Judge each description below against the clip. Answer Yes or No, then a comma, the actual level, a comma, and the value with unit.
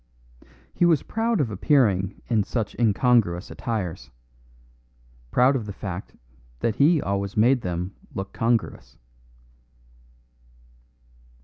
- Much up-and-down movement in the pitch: No, average, 4.8 semitones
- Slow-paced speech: Yes, slow, 105 wpm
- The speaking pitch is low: Yes, low, 110 Hz